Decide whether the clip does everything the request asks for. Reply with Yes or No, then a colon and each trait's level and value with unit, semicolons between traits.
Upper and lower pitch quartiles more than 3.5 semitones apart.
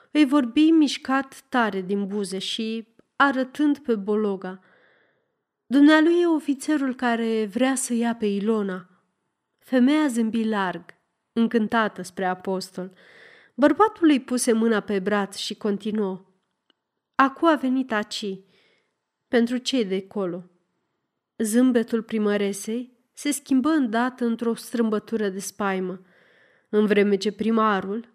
Yes: average, 4.4 semitones